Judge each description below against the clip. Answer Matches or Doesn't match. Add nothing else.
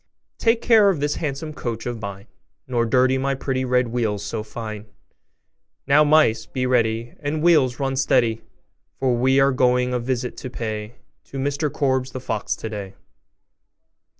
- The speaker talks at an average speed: Matches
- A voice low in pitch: Matches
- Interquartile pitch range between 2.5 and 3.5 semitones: Matches